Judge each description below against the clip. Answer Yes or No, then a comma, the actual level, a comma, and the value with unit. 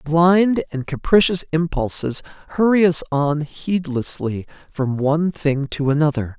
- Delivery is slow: Yes, slow, 120 wpm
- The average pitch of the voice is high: No, medium, 155 Hz